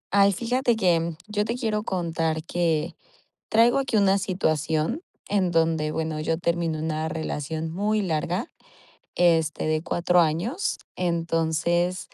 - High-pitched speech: No, medium, 170 Hz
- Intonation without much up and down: No, average, 3.8 semitones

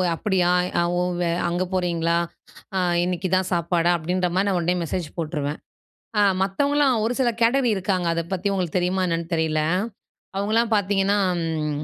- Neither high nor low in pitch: Yes, medium, 180 Hz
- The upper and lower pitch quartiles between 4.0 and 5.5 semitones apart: No, average, 2.8 semitones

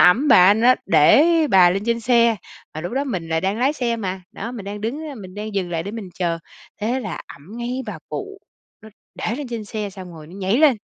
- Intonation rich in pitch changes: No, average, 4.6 semitones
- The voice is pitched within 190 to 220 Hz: Yes, high, 215 Hz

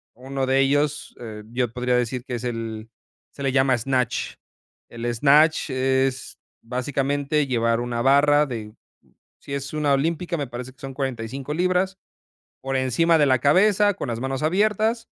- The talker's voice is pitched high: No, low, 135 Hz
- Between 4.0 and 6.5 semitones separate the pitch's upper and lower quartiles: No, average, 3.3 semitones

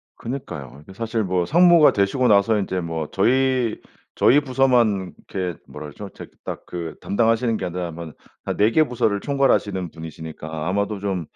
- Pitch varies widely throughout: Yes, wide, 6.0 semitones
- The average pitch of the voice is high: No, low, 100 Hz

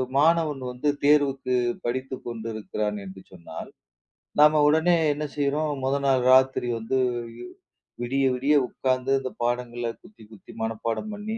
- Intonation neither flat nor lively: Yes, average, 3.7 semitones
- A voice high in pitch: No, low, 130 Hz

